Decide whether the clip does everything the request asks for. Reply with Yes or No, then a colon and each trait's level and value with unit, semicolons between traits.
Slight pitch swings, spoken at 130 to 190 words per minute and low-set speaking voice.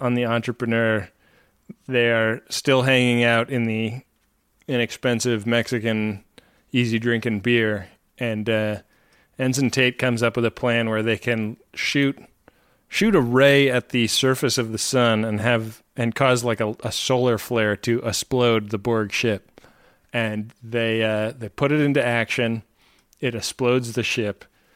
Yes: narrow, 2.0 semitones; average, 155 wpm; low, 120 Hz